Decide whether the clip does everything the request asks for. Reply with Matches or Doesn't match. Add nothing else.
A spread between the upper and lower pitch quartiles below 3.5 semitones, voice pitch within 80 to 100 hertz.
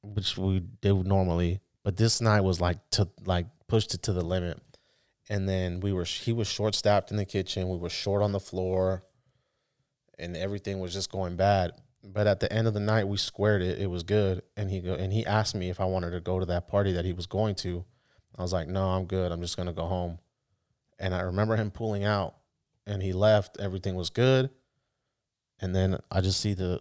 Matches